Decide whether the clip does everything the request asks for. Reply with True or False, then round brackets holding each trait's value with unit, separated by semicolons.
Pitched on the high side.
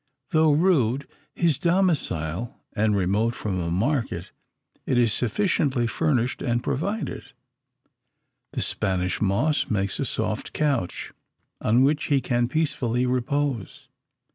False (125 Hz)